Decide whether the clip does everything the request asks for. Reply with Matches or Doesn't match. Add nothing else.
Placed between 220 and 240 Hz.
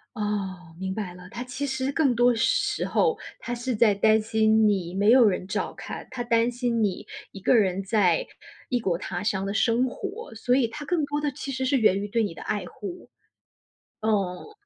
Matches